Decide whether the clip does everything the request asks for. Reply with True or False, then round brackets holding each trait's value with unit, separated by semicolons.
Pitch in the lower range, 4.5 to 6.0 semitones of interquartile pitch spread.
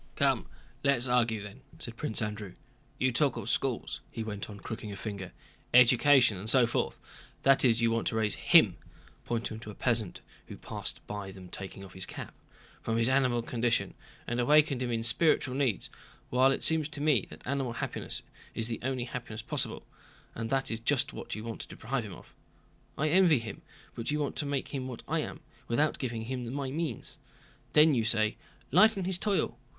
False (120 Hz; 3.6 semitones)